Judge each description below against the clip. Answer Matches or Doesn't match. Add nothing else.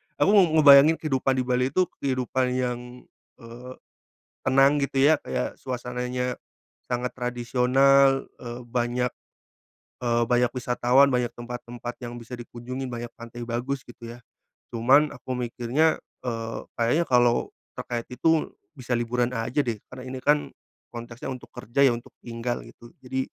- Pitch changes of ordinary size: Doesn't match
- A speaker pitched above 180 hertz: Doesn't match